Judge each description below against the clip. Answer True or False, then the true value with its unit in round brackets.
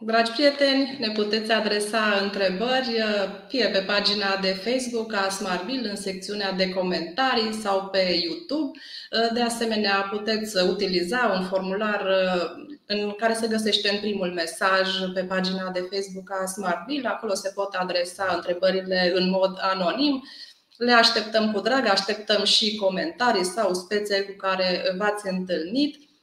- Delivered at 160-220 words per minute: False (140 wpm)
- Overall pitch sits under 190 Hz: False (200 Hz)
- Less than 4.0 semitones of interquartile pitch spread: True (3.1 semitones)